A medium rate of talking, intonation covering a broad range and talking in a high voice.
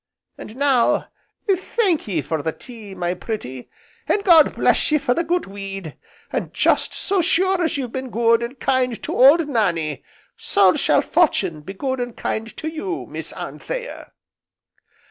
Yes: average, 165 wpm; wide, 8.6 semitones; very high, 250 Hz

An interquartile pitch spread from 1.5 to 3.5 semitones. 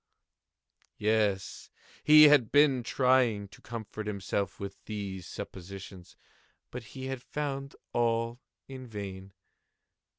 No: average, 4.8 semitones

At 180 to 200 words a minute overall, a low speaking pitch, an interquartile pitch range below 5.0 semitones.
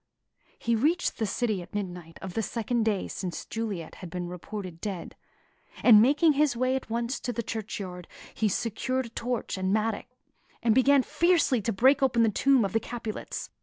No: average, 185 wpm; high, 225 Hz; average, 4.6 semitones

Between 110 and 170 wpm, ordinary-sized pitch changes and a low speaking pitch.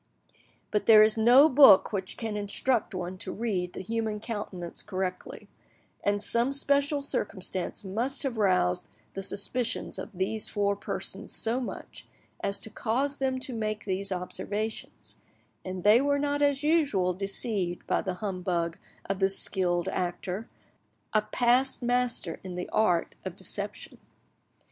No: average, 145 wpm; average, 4.7 semitones; high, 210 Hz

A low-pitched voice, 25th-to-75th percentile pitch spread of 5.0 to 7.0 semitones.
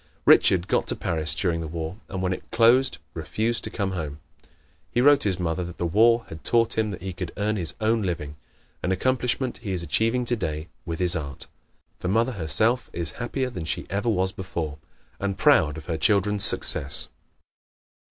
Yes: very low, 95 Hz; wide, 5.5 semitones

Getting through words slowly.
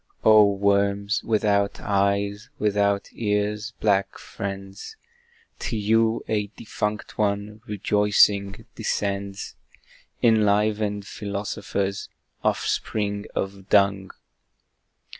Yes: slow, 80 wpm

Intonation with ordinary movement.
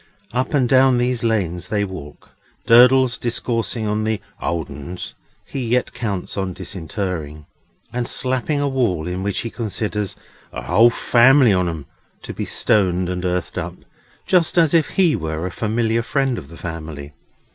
No: wide, 5.7 semitones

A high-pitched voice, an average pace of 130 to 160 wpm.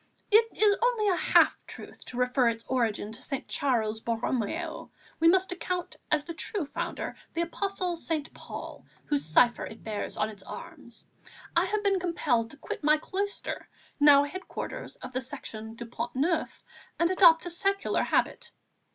No: very high, 300 Hz; average, 170 wpm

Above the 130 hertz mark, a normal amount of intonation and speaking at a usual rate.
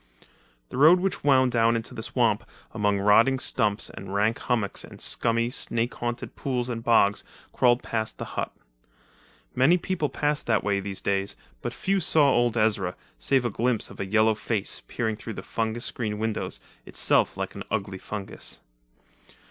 No: low, 115 Hz; average, 3.1 semitones; average, 170 wpm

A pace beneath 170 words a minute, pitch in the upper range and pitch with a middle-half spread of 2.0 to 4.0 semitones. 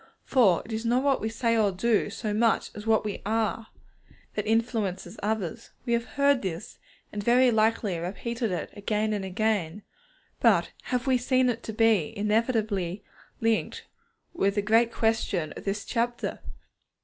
Yes: average, 160 wpm; high, 220 Hz; narrow, 2.5 semitones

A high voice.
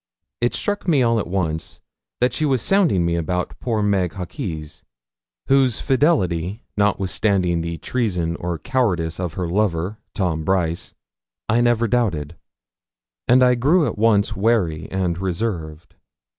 No: very low, 95 Hz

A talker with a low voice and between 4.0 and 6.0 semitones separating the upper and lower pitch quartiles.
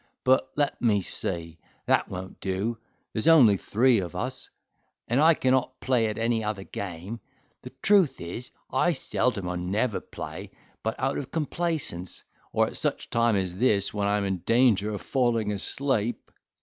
Yes: low, 115 Hz; average, 4.9 semitones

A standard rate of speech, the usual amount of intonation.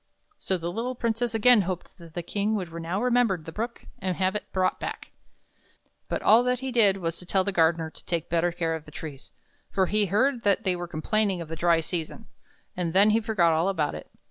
No: fast, 225 wpm; average, 4.4 semitones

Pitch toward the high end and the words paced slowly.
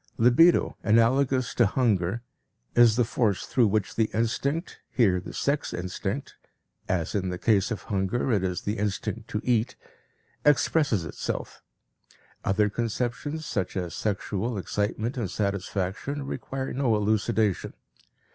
No: low, 110 Hz; slow, 130 wpm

